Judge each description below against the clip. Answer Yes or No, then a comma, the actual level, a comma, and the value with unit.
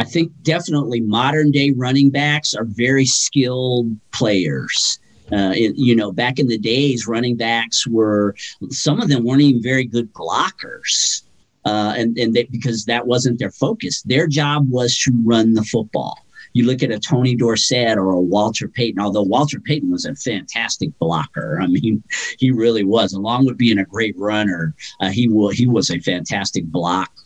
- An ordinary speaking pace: Yes, average, 180 wpm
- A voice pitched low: Yes, low, 120 Hz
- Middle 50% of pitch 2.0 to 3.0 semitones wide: No, average, 3.4 semitones